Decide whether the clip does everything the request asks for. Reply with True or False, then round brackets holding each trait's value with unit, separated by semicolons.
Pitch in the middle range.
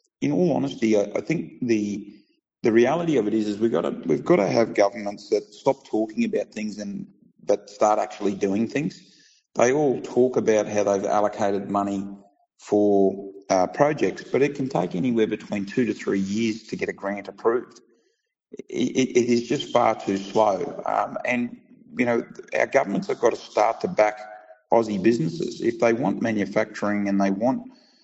False (105 Hz)